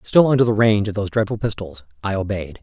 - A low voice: Yes, low, 105 Hz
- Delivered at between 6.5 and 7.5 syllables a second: Yes, 6.8 syllables/s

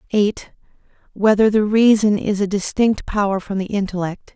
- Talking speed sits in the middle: Yes, average, 150 wpm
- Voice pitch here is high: Yes, high, 205 Hz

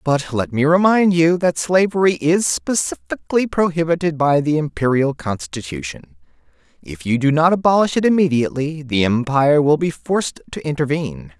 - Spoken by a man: Yes, male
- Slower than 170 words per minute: Yes, average, 145 wpm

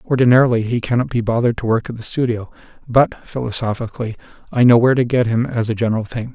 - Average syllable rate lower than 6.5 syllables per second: No, 6.9 syllables/s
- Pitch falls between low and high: No, low, 120 Hz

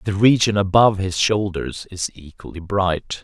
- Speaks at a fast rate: No, average, 150 wpm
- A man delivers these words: Yes, male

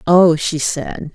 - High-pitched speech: No, medium, 155 Hz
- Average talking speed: Yes, average, 160 wpm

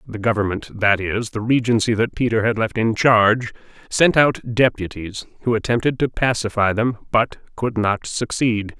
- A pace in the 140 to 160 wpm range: Yes, average, 150 wpm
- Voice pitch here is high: No, low, 110 Hz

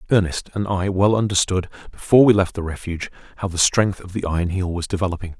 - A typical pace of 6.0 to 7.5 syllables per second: Yes, 6.6 syllables/s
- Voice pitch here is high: No, very low, 95 Hz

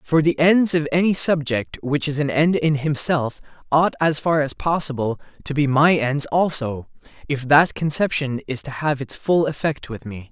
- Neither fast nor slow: Yes, average, 190 wpm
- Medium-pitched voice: Yes, medium, 145 Hz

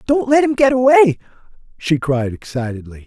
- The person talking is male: Yes, male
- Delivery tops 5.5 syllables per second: Yes, 5.9 syllables/s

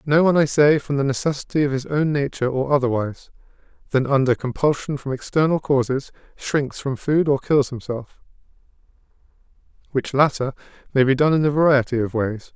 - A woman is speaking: No, male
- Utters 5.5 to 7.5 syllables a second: Yes, 5.7 syllables/s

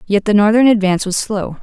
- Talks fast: Yes, fast, 220 wpm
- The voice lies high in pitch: Yes, high, 205 Hz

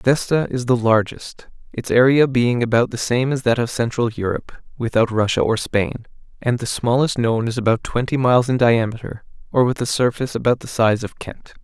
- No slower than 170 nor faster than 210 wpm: Yes, average, 185 wpm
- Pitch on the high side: No, low, 120 Hz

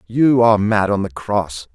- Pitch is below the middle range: Yes, low, 105 Hz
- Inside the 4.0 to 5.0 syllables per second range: Yes, 4.5 syllables/s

